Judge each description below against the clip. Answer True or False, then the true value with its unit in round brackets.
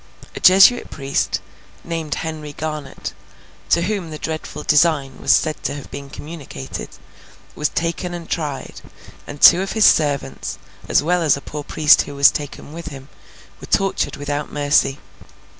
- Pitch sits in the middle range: True (150 Hz)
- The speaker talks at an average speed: True (160 wpm)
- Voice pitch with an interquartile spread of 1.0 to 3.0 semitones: True (2.7 semitones)